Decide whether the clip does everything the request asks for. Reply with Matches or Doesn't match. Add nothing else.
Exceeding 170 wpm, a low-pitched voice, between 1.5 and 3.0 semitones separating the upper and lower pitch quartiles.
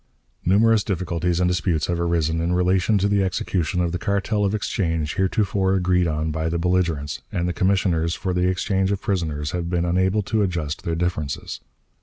Matches